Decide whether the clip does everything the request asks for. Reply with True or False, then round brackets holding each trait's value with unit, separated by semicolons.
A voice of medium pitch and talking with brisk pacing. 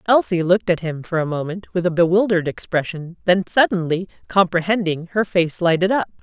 False (180 Hz; 175 wpm)